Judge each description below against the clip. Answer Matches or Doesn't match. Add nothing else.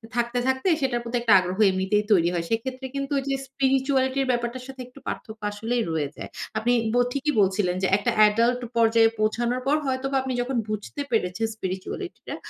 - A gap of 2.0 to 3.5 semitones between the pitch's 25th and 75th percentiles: Doesn't match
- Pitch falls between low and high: Doesn't match